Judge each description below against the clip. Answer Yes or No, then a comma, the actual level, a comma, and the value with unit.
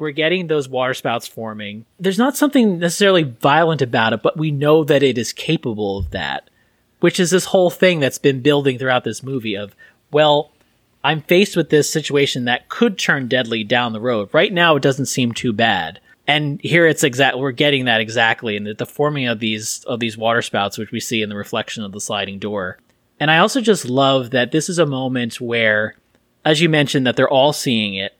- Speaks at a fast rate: Yes, fast, 210 wpm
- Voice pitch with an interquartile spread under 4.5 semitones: No, average, 5.3 semitones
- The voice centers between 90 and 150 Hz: Yes, low, 135 Hz